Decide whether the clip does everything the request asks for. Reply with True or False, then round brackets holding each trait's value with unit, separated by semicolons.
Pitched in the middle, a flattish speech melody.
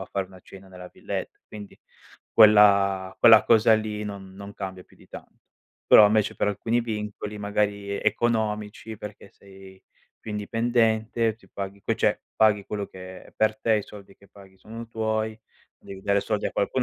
False (105 Hz; 1.9 semitones)